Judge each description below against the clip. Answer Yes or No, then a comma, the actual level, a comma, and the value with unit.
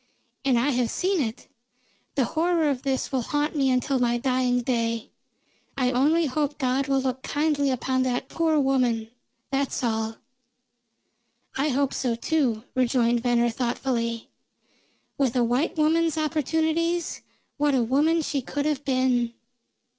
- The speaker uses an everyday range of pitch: Yes, average, 3.3 semitones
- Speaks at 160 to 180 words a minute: No, average, 145 wpm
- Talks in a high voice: Yes, very high, 265 Hz